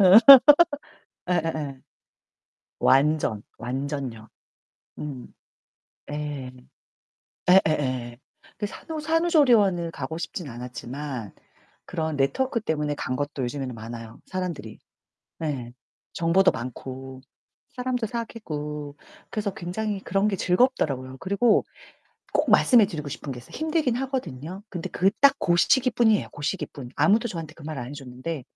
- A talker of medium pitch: Yes, medium, 155 Hz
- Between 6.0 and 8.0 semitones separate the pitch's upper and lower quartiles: Yes, wide, 7.3 semitones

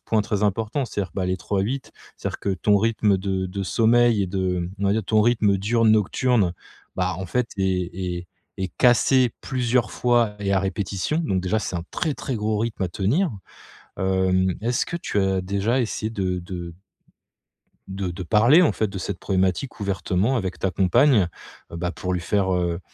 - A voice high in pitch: No, low, 100 Hz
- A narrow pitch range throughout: No, average, 3.6 semitones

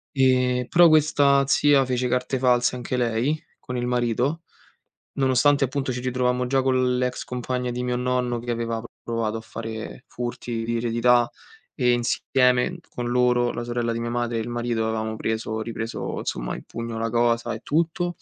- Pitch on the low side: Yes, low, 125 Hz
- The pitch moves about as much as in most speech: No, narrow, 1.5 semitones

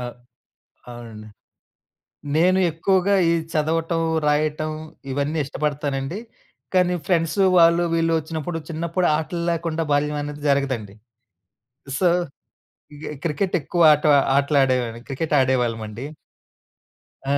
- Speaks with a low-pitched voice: No, medium, 155 Hz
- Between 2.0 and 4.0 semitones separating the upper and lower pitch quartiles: Yes, average, 3.4 semitones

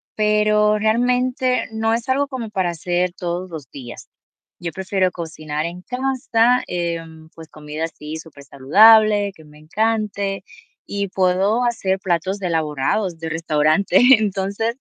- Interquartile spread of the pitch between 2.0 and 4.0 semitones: No, average, 5.1 semitones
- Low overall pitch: No, high, 190 Hz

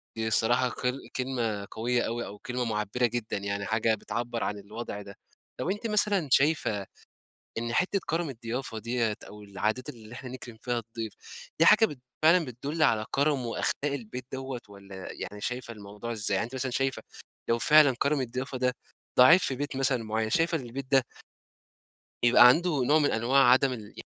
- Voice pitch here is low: Yes, low, 120 Hz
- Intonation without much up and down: No, average, 3.5 semitones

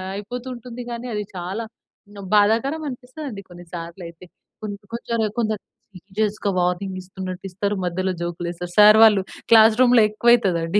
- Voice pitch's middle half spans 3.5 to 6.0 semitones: Yes, average, 4.3 semitones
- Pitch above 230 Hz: No, high, 205 Hz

